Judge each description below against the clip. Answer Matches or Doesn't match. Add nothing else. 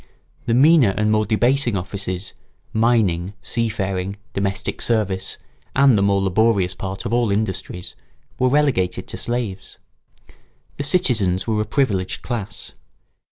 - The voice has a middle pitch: Doesn't match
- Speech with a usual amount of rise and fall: Matches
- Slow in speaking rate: Matches